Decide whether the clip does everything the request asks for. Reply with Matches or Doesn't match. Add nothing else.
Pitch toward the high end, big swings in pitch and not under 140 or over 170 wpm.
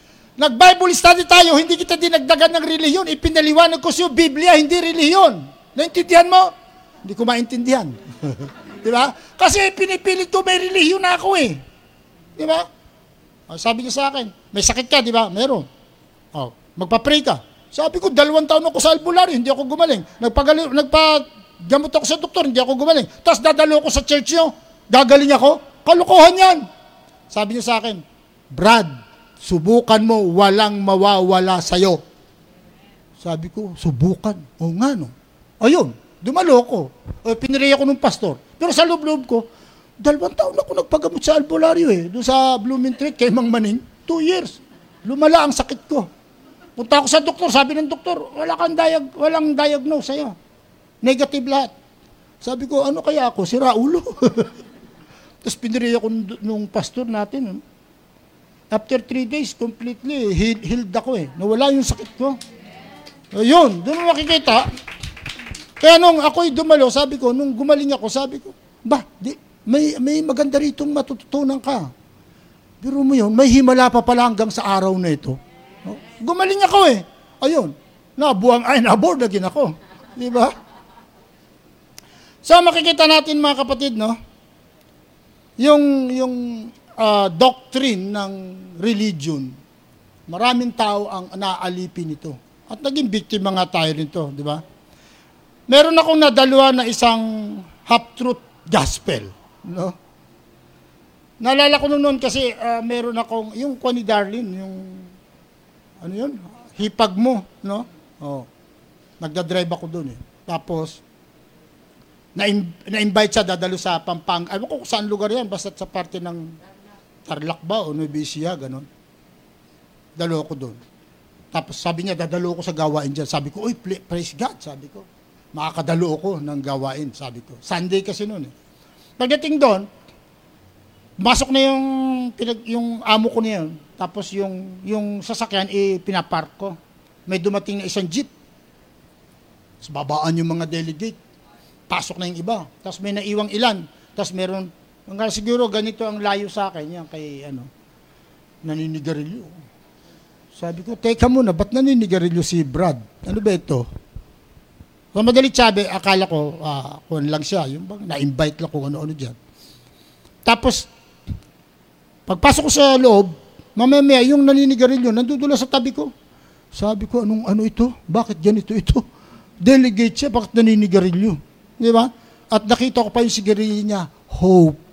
Matches